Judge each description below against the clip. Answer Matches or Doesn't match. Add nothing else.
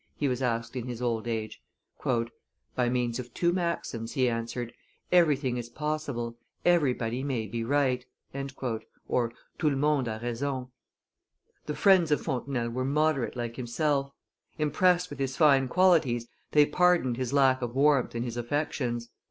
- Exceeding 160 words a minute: Doesn't match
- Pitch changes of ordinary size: Matches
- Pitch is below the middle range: Matches